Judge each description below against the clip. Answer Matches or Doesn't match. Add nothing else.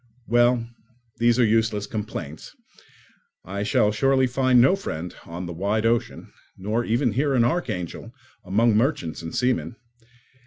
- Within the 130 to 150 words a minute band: Matches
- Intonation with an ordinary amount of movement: Matches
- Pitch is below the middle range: Matches